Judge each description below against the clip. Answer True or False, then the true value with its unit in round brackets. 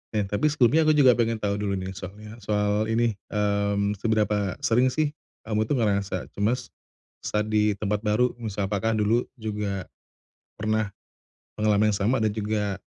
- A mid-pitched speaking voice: False (105 Hz)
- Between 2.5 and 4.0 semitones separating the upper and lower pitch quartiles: False (1.7 semitones)